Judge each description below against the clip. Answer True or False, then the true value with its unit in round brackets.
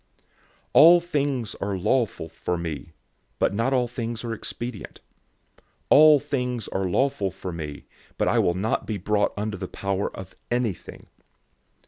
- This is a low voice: True (110 Hz)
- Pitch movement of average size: True (4.8 semitones)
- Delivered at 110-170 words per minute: True (150 wpm)